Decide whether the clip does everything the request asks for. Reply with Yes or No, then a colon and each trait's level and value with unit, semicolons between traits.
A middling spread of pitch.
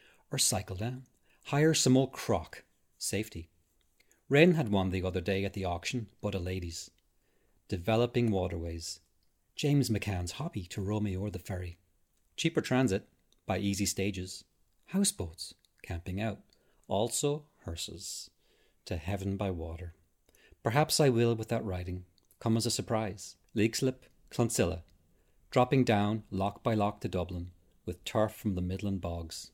Yes: average, 4.7 semitones